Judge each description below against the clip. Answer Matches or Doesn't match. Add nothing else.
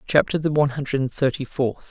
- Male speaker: Matches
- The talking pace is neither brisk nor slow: Doesn't match